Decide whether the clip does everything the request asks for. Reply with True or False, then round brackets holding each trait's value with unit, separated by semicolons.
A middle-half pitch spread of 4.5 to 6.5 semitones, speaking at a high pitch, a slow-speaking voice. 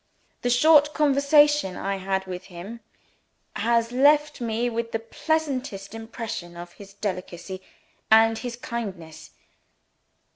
True (5.4 semitones; 225 Hz; 115 wpm)